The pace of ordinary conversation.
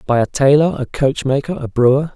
Yes: average, 195 wpm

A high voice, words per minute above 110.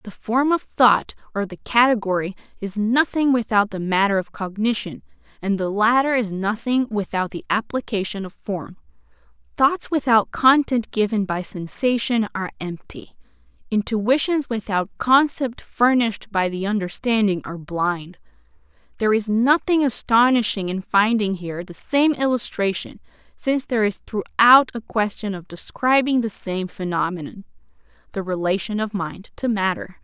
Yes: high, 215 Hz; slow, 135 wpm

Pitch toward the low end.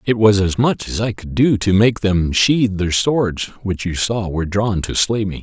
Yes: low, 100 Hz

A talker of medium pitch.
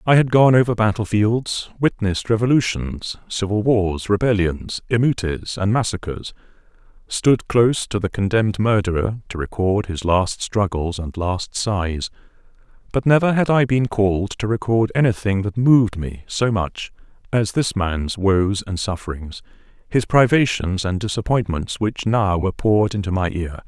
No: low, 105 Hz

